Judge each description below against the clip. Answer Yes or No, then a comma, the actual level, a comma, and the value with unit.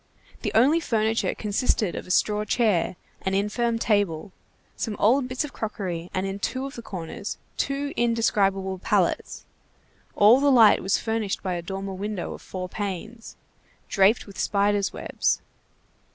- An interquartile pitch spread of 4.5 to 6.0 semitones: No, average, 3.2 semitones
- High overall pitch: Yes, high, 210 Hz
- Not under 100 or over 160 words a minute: Yes, average, 150 wpm